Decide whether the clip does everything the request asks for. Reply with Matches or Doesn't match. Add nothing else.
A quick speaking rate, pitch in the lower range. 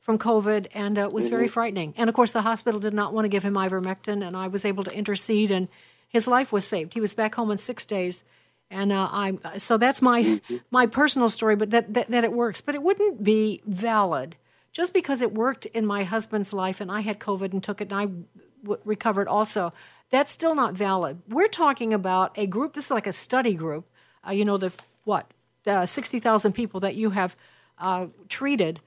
Doesn't match